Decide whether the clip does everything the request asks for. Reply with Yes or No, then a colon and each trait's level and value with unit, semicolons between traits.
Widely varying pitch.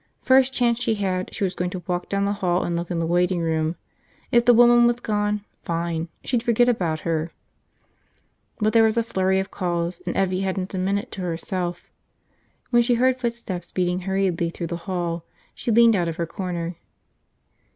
No: average, 4.7 semitones